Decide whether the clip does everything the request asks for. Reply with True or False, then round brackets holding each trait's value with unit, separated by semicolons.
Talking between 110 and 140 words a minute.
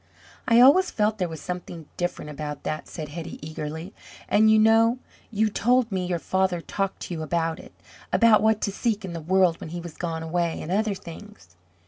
False (200 wpm)